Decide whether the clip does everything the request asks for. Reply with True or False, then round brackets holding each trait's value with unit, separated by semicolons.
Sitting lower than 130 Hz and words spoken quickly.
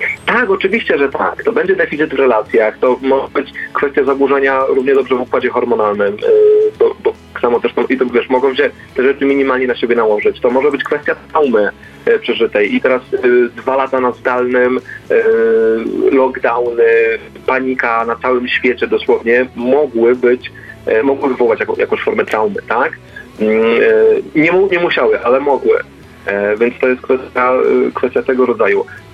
False (140 Hz; 165 wpm)